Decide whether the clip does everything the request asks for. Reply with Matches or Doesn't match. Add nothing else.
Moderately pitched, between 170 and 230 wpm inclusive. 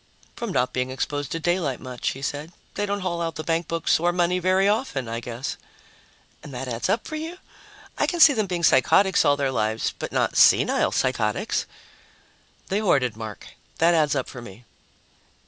Matches